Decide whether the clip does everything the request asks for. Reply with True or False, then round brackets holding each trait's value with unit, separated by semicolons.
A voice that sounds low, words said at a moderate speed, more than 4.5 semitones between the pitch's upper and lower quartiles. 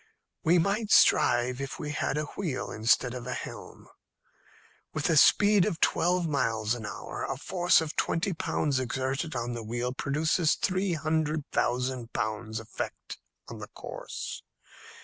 False (145 Hz; 150 wpm; 5.2 semitones)